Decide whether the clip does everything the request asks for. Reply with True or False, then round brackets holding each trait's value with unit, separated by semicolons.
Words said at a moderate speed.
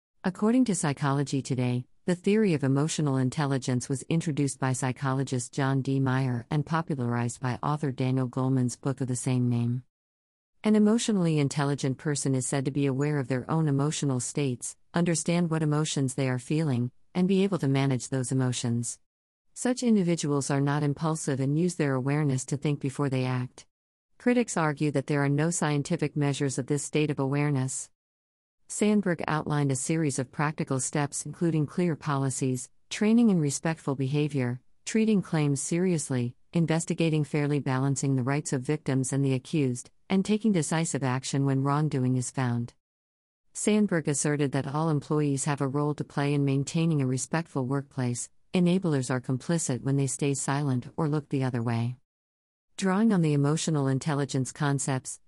True (160 wpm)